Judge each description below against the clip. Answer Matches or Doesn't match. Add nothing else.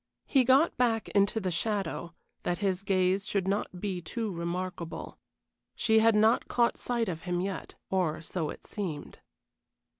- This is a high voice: Matches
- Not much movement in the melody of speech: Doesn't match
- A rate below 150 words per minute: Doesn't match